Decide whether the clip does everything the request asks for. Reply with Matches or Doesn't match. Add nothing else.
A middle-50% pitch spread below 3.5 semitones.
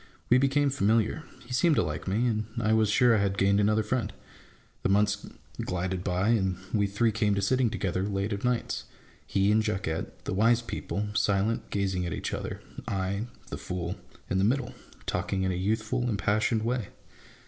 Matches